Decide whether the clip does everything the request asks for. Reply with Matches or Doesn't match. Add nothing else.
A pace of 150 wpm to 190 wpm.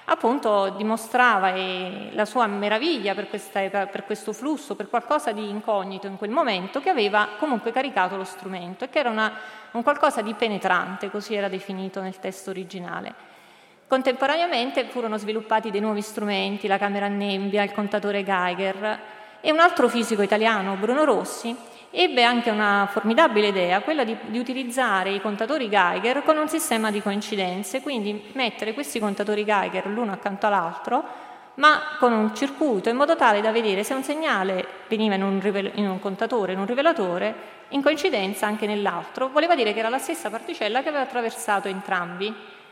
Matches